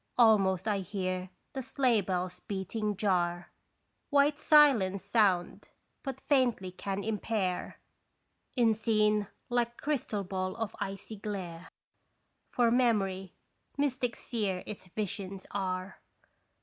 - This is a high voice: Yes, high, 205 Hz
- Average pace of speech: No, slow, 110 wpm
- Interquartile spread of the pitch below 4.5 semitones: Yes, average, 3.9 semitones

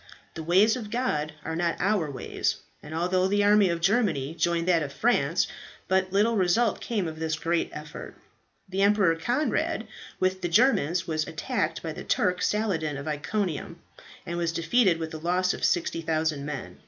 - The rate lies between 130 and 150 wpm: No, average, 175 wpm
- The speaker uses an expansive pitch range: No, average, 4.0 semitones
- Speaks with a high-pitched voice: No, medium, 175 Hz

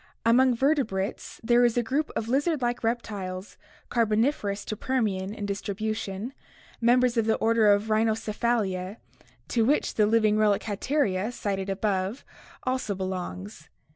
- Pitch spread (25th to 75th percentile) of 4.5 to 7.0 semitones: No, average, 3.3 semitones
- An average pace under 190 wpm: Yes, average, 140 wpm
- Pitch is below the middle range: No, high, 220 Hz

